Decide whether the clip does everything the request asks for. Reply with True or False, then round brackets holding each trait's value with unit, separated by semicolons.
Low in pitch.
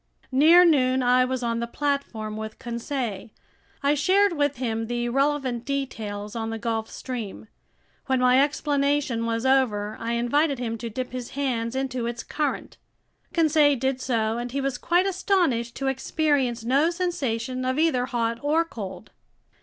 False (255 Hz)